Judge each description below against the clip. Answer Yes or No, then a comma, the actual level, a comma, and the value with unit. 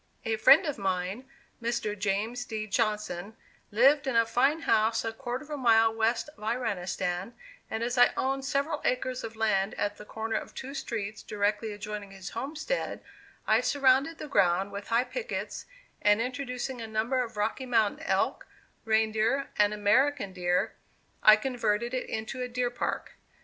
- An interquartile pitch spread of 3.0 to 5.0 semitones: Yes, average, 3.4 semitones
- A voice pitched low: No, high, 225 Hz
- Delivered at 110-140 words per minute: No, average, 165 wpm